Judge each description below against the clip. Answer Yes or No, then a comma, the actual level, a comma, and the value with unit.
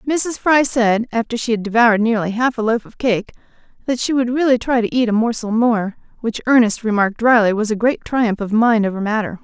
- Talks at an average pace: No, fast, 225 wpm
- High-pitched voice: Yes, high, 230 Hz